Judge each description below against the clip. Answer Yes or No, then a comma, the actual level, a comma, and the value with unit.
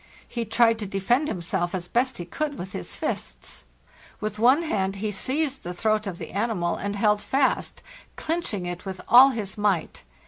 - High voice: Yes, high, 210 Hz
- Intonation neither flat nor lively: Yes, average, 4.6 semitones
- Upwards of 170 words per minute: Yes, average, 180 wpm